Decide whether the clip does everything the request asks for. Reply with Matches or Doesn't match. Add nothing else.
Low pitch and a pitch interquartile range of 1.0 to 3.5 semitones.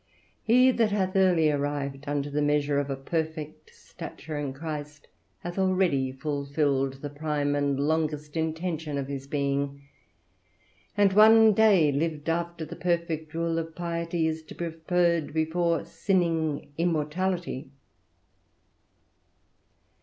Doesn't match